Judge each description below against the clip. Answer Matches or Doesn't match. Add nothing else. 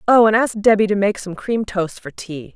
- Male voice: Doesn't match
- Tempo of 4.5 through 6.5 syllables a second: Matches